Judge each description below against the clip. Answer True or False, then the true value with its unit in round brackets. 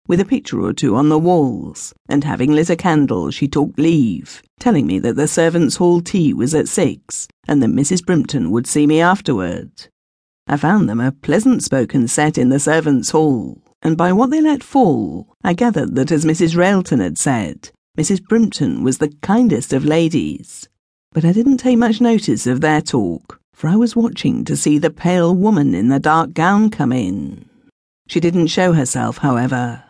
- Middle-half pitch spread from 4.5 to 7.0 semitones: True (5.0 semitones)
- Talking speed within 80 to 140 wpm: False (190 wpm)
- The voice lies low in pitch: False (160 Hz)